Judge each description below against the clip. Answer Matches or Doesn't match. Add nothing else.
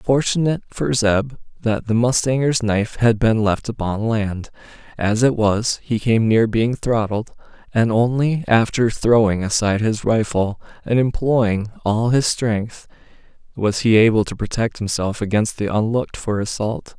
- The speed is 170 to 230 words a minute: Doesn't match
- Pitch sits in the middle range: Doesn't match